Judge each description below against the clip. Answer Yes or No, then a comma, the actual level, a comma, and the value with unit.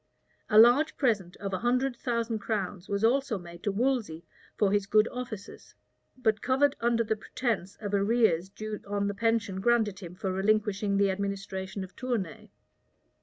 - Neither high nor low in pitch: No, high, 210 Hz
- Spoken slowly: No, average, 165 wpm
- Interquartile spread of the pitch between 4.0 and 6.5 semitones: No, average, 3.3 semitones